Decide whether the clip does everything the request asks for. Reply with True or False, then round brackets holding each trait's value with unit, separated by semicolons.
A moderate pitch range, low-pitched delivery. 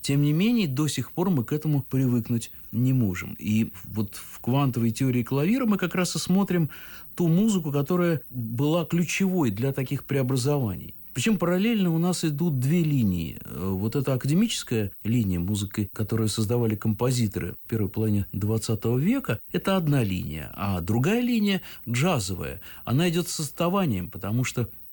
False (7.6 semitones; 130 Hz)